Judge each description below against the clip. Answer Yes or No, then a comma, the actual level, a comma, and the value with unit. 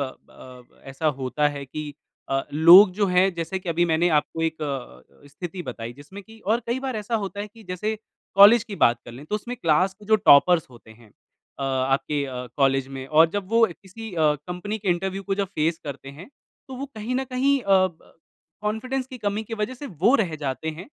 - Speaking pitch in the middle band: Yes, medium, 180 Hz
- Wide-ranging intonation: Yes, wide, 6.8 semitones